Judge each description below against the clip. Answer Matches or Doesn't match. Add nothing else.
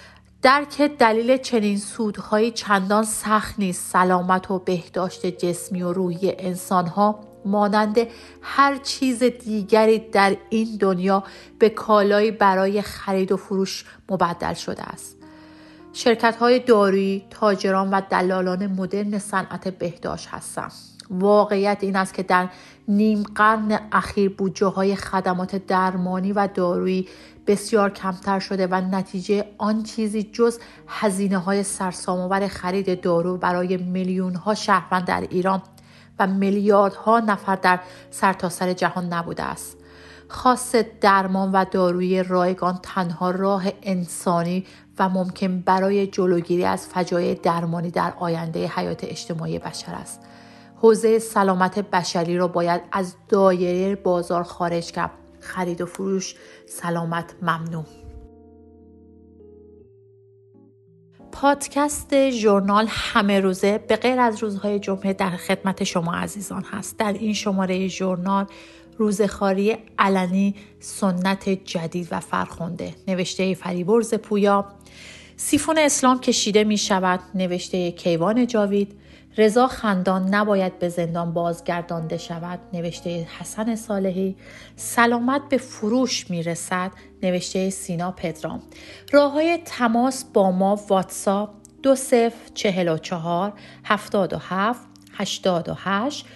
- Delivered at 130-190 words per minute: Doesn't match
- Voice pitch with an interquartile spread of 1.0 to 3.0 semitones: Matches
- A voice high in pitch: Matches